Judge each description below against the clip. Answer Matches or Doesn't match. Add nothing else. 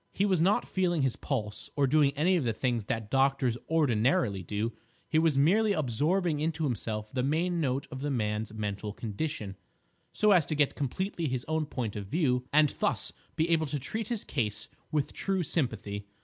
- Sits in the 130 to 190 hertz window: Matches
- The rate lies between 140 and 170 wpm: Doesn't match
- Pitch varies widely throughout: Matches